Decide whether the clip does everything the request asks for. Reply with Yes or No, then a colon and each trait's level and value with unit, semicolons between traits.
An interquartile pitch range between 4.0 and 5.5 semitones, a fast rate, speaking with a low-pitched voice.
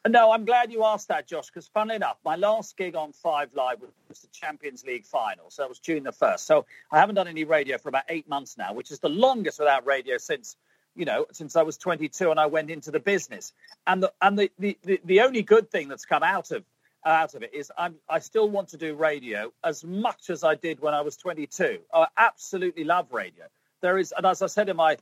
No: average, 4.7 semitones; fast, 250 wpm; medium, 175 Hz